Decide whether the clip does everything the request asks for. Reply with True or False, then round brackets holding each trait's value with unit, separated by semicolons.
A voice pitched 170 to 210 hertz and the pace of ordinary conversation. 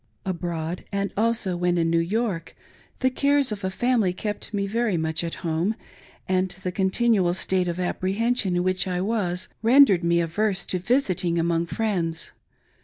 True (185 Hz; 170 wpm)